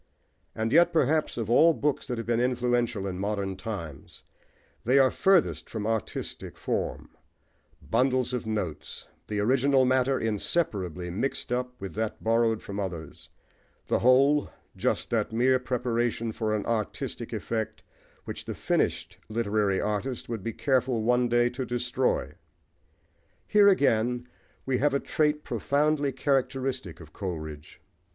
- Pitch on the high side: No, low, 120 Hz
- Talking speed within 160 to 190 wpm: No, average, 140 wpm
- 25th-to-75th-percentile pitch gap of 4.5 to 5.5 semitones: No, average, 3.7 semitones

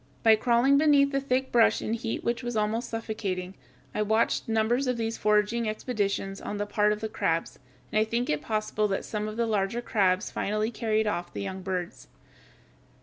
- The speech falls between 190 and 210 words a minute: Yes, average, 195 wpm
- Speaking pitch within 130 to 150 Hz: No, high, 215 Hz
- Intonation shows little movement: Yes, narrow, 2.3 semitones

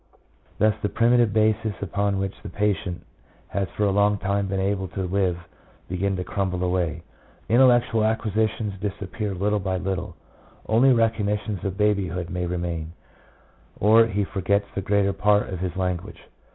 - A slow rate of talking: No, average, 160 wpm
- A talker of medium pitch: No, low, 100 Hz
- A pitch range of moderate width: No, narrow, 2.2 semitones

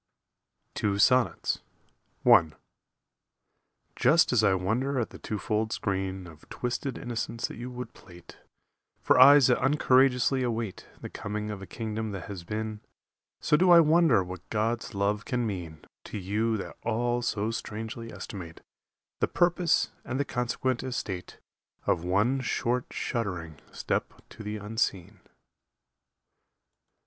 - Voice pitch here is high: No, low, 110 Hz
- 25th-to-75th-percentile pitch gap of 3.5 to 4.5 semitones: Yes, average, 3.9 semitones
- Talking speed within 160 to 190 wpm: No, slow, 135 wpm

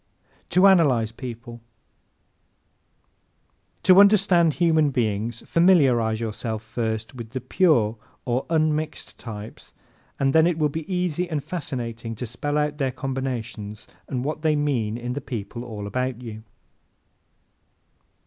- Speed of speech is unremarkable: No, slow, 130 wpm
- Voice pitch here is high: No, low, 130 Hz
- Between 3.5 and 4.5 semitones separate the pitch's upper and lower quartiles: No, wide, 5.5 semitones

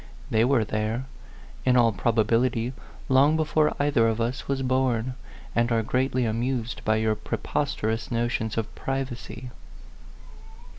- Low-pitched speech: Yes, low, 120 Hz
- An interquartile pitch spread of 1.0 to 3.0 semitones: Yes, narrow, 2.6 semitones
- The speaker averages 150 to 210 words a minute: No, slow, 135 wpm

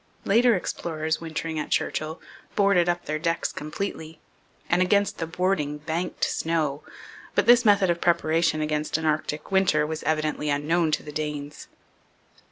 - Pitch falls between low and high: Yes, medium, 160 Hz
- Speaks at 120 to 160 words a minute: Yes, average, 150 wpm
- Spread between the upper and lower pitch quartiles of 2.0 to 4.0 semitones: Yes, average, 2.7 semitones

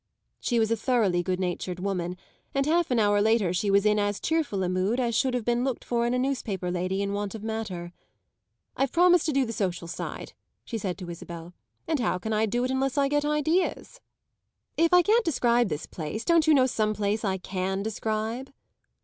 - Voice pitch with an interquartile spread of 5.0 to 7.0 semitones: Yes, wide, 5.5 semitones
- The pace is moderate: No, fast, 215 wpm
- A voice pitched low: No, high, 220 Hz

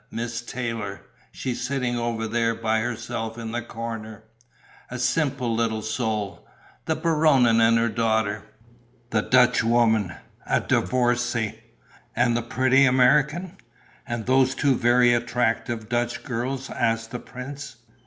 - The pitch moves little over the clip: Yes, narrow, 2.0 semitones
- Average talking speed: No, slow, 125 wpm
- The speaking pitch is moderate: No, low, 120 Hz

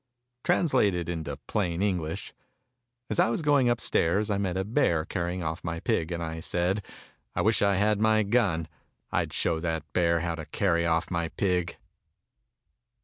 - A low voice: Yes, very low, 90 Hz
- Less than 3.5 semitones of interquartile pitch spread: No, average, 3.8 semitones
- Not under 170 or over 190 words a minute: Yes, average, 175 wpm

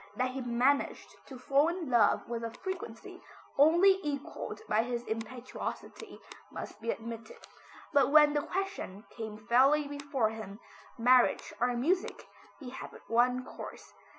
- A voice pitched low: No, very high, 255 Hz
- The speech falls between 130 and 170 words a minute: Yes, average, 145 wpm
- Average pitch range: Yes, average, 4.3 semitones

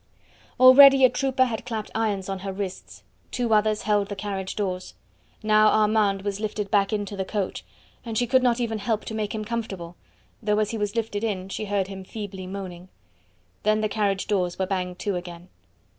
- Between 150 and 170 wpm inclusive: No, average, 195 wpm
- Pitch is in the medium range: No, high, 210 Hz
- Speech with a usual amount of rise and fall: No, narrow, 2.3 semitones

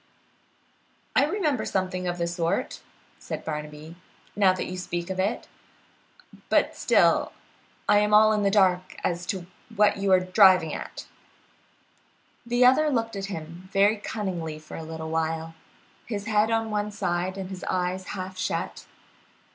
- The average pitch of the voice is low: No, medium, 185 Hz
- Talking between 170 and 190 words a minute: No, average, 155 wpm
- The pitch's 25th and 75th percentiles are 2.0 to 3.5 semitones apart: Yes, average, 3.1 semitones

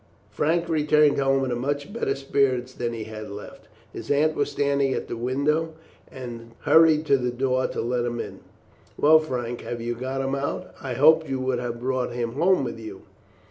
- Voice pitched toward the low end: Yes, low, 130 Hz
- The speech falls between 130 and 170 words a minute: No, average, 195 wpm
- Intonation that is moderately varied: Yes, average, 3.4 semitones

